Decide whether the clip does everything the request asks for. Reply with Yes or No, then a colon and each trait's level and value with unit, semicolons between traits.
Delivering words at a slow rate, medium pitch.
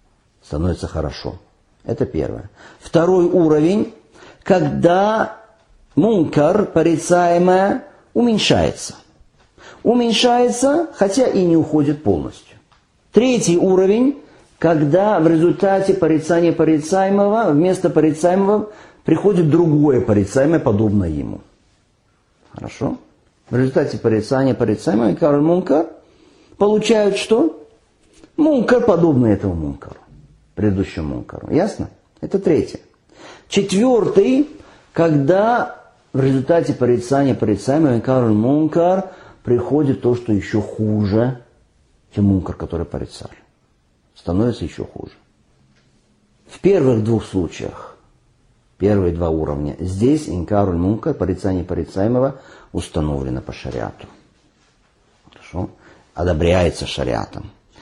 Yes: slow, 90 wpm; medium, 145 Hz